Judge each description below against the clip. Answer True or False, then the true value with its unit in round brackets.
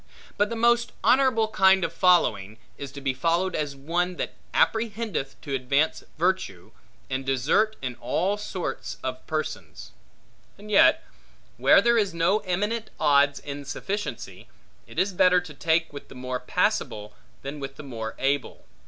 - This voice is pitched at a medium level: True (165 Hz)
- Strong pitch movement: True (7.1 semitones)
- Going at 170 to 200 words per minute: False (155 wpm)